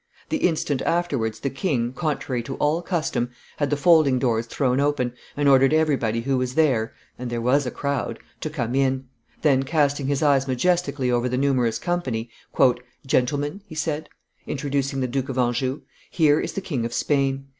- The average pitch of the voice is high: No, low, 135 Hz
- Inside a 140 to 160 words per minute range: No, average, 175 wpm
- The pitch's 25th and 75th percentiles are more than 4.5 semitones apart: No, average, 3.0 semitones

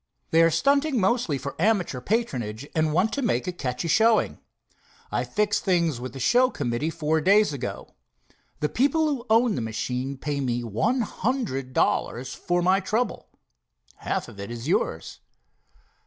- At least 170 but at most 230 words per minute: No, average, 160 wpm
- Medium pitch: Yes, medium, 165 Hz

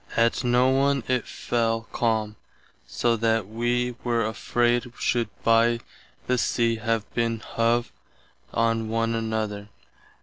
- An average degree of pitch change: No, narrow, 1.1 semitones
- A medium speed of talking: No, slow, 115 wpm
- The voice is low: Yes, low, 115 Hz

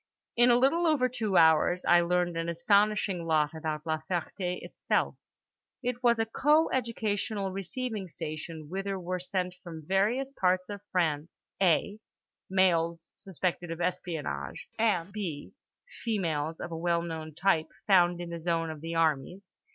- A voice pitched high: No, medium, 180 Hz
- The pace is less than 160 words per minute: Yes, average, 150 wpm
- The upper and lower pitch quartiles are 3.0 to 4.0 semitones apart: Yes, average, 3.6 semitones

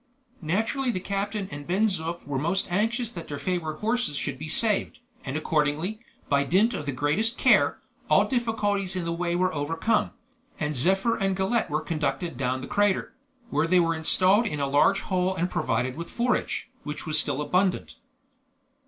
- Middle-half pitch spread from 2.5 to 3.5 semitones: No, average, 5.3 semitones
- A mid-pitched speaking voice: Yes, medium, 180 Hz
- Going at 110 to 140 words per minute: No, average, 180 wpm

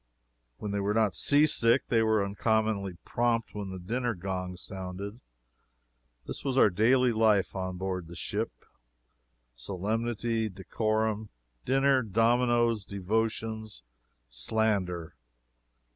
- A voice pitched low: Yes, low, 110 Hz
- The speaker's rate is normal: No, slow, 110 wpm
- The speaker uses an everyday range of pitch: Yes, average, 3.4 semitones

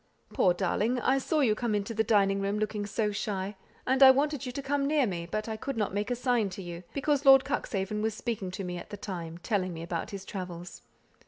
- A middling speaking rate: No, fast, 240 wpm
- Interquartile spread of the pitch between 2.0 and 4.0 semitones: No, average, 4.8 semitones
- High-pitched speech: Yes, high, 210 Hz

